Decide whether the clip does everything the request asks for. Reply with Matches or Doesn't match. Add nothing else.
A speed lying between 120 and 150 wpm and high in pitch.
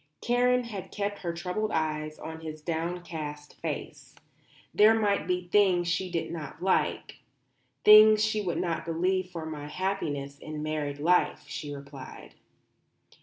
Doesn't match